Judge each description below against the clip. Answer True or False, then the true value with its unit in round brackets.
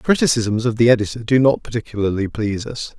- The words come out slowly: False (200 wpm)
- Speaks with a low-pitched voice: True (115 Hz)